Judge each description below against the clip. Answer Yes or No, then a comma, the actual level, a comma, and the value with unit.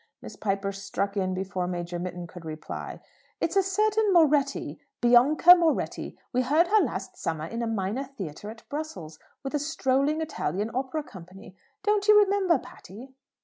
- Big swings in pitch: Yes, wide, 8.8 semitones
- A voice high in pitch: Yes, high, 245 Hz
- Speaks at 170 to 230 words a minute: No, average, 160 wpm